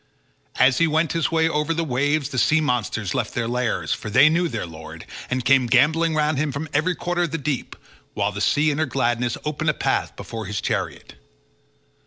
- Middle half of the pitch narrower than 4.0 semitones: No, average, 4.4 semitones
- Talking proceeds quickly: Yes, fast, 210 wpm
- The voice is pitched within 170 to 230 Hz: No, medium, 145 Hz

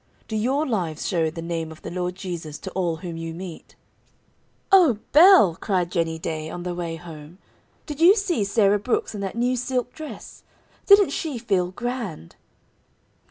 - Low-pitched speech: No, high, 190 Hz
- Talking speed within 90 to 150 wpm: No, average, 170 wpm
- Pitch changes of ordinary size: No, wide, 7.0 semitones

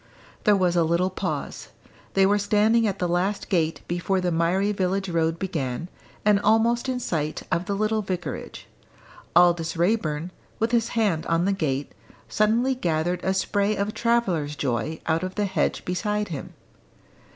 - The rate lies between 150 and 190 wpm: Yes, average, 160 wpm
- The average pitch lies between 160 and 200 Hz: Yes, medium, 185 Hz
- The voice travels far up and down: No, average, 3.8 semitones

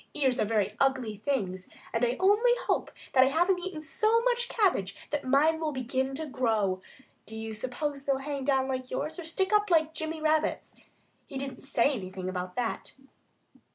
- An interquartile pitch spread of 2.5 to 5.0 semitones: No, wide, 5.4 semitones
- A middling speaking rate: Yes, average, 185 wpm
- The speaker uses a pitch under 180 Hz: No, very high, 275 Hz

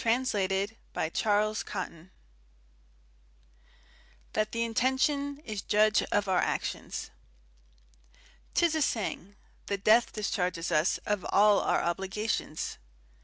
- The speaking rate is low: Yes, slow, 100 wpm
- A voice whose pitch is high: Yes, high, 210 Hz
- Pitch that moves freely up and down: No, average, 3.0 semitones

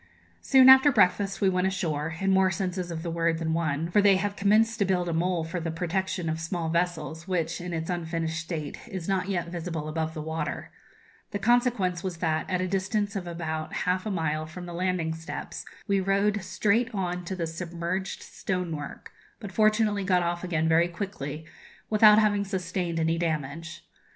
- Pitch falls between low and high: Yes, medium, 180 Hz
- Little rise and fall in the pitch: No, average, 3.0 semitones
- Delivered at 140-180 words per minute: No, average, 190 wpm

